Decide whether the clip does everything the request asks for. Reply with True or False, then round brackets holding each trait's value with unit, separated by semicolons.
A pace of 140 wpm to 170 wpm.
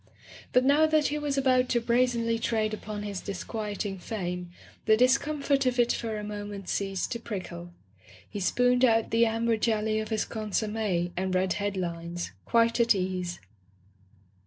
True (160 wpm)